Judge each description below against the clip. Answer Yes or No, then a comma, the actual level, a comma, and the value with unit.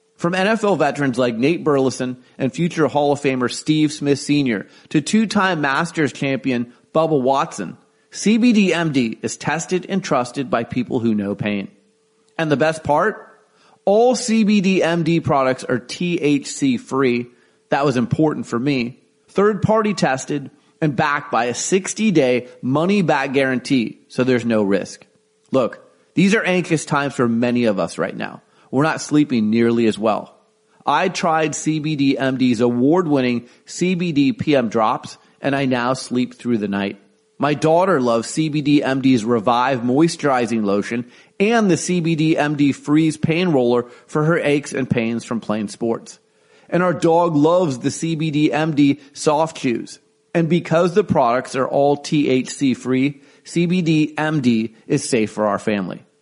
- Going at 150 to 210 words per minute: No, average, 140 wpm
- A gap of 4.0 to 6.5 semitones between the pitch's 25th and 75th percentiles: Yes, average, 4.9 semitones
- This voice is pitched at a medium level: Yes, medium, 145 Hz